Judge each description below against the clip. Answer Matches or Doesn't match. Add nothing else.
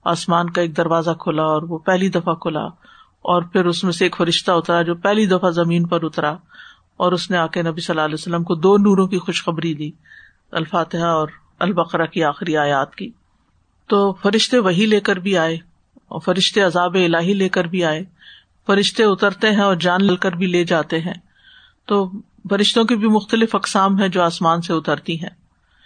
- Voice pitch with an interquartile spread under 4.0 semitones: Matches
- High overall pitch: Doesn't match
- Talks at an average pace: Doesn't match